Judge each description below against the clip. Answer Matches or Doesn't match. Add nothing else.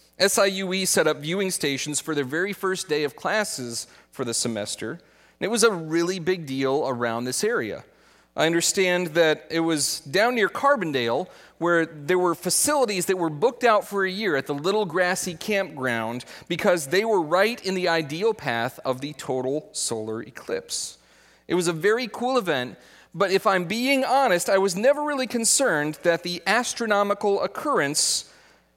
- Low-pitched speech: Doesn't match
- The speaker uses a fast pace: Doesn't match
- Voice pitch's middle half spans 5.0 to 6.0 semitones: Matches